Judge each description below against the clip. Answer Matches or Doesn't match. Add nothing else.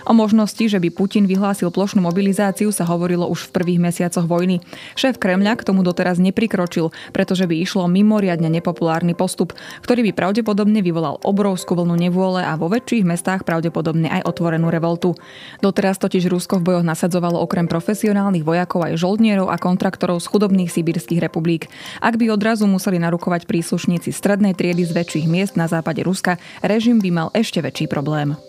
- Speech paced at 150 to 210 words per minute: Matches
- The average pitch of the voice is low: Doesn't match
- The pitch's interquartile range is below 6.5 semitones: Matches